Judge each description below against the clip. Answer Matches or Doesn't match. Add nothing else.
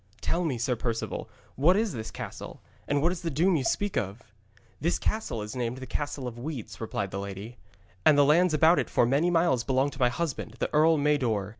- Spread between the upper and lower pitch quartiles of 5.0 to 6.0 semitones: Matches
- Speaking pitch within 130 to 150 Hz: Matches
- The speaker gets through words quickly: Matches